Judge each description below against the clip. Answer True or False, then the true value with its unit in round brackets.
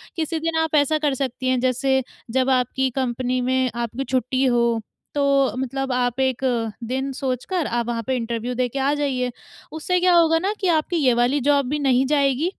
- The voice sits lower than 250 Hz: False (265 Hz)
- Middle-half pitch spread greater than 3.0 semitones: False (2.7 semitones)